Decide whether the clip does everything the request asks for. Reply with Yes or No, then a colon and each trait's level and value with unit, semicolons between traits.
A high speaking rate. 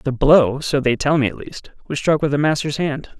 Yes: fast, 265 wpm